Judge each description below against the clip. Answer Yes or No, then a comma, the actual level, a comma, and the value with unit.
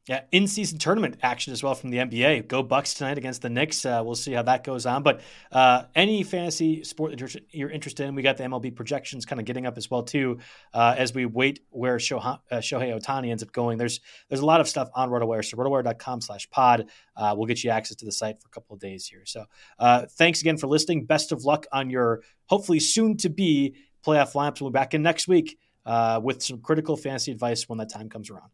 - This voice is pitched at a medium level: No, low, 130 Hz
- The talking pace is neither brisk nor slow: No, fast, 240 wpm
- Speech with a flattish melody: No, average, 4.1 semitones